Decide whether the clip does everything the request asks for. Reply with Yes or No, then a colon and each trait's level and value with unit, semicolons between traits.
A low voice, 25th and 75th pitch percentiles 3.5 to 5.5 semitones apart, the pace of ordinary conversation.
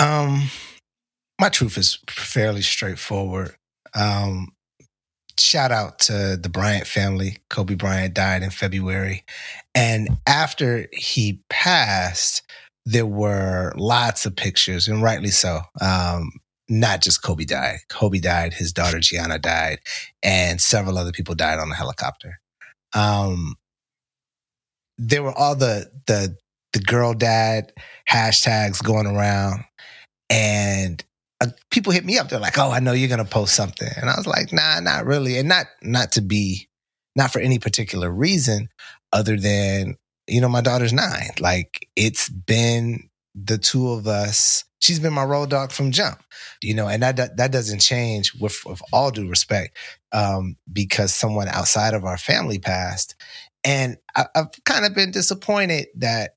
Yes: low, 105 Hz; average, 4.6 semitones; average, 150 wpm